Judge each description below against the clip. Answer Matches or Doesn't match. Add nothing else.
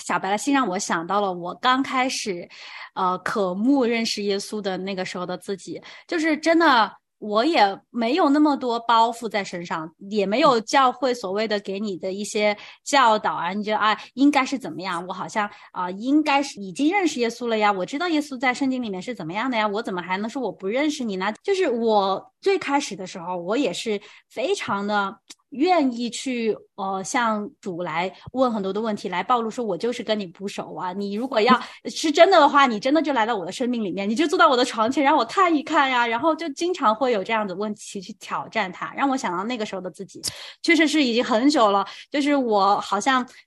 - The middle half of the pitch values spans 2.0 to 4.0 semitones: Doesn't match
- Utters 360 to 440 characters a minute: Doesn't match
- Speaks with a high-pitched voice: Matches